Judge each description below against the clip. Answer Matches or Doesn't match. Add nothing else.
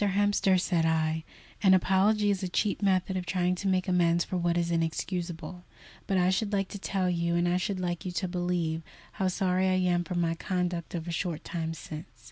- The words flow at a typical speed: Doesn't match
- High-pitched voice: Doesn't match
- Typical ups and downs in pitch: Doesn't match